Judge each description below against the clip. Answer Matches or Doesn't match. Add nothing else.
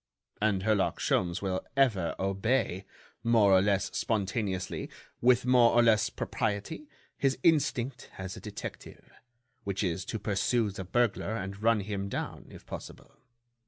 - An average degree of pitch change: Matches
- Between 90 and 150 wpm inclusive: Matches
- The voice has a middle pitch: Doesn't match